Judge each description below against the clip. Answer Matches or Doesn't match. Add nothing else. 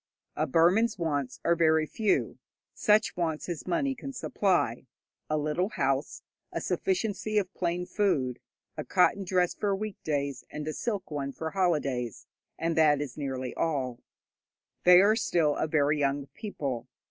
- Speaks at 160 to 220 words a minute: Doesn't match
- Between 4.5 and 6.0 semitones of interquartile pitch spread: Matches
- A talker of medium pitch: Matches